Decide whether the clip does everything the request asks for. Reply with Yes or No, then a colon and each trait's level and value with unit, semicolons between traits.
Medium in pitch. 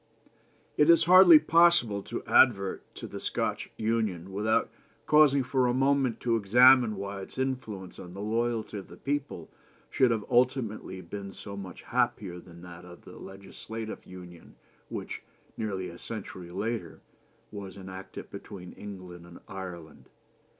No: low, 105 Hz